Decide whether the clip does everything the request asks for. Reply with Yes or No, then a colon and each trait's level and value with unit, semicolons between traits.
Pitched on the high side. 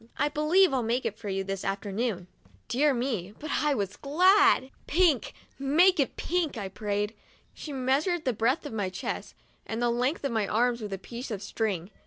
Yes: high, 240 Hz